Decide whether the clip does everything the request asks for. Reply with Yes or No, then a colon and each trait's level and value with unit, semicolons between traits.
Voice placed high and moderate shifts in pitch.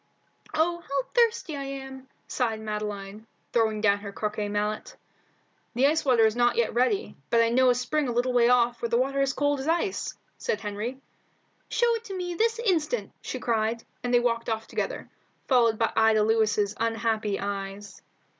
Yes: high, 235 Hz; average, 4.2 semitones